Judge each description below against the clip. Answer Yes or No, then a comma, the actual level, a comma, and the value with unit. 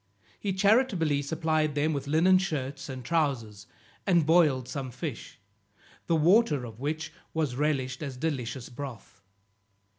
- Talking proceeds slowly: Yes, slow, 130 wpm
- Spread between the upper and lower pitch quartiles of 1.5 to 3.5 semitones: No, average, 3.9 semitones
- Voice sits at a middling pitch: Yes, medium, 145 Hz